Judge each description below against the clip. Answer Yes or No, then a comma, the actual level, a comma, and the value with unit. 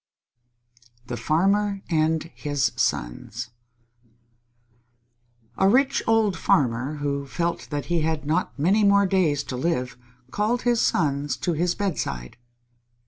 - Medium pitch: Yes, medium, 160 Hz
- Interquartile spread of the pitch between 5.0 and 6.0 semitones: Yes, wide, 5.6 semitones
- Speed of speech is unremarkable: No, slow, 125 wpm